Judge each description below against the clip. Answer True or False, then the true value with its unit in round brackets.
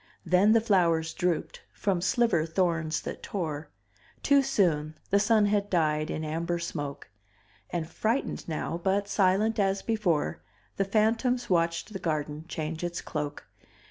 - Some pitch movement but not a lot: True (4.4 semitones)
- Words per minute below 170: True (140 wpm)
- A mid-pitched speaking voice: True (175 Hz)